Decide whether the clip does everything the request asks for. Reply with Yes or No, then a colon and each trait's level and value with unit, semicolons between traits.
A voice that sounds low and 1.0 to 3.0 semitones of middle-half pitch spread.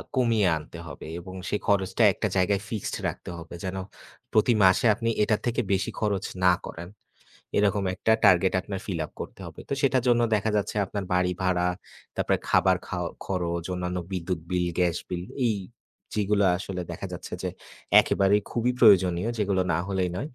Yes: very low, 95 Hz; narrow, 2.6 semitones